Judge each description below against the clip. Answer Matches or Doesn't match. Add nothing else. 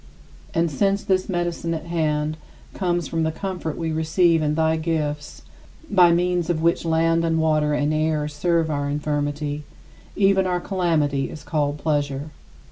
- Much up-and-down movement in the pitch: Doesn't match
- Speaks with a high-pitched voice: Doesn't match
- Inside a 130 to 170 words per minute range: Matches